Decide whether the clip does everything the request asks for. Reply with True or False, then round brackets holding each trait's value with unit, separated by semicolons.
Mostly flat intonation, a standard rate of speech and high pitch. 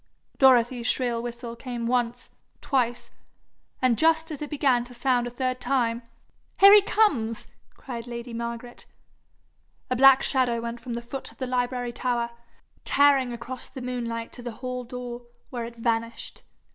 True (1.7 semitones; 160 wpm; 245 Hz)